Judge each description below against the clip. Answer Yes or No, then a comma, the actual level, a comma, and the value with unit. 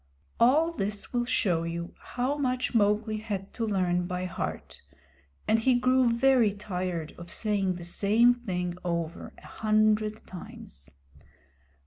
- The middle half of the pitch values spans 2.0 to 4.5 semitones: No, average, 4.9 semitones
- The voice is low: No, high, 210 Hz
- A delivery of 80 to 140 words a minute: Yes, slow, 135 wpm